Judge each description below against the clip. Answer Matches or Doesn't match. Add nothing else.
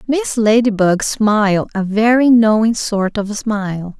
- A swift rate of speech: Doesn't match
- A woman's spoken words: Matches